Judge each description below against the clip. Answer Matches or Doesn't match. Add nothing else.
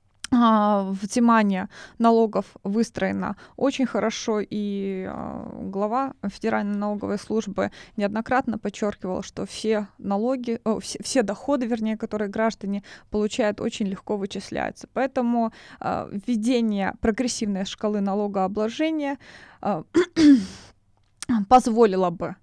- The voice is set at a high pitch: Matches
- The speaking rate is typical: Doesn't match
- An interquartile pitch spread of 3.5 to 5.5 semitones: Doesn't match